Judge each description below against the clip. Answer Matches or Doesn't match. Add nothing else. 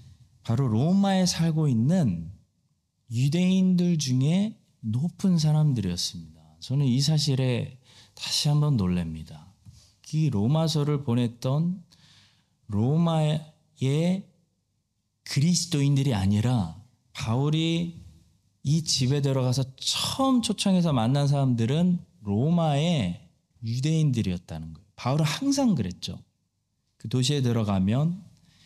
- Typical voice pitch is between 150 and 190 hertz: Doesn't match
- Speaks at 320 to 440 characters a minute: Doesn't match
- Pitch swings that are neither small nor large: Doesn't match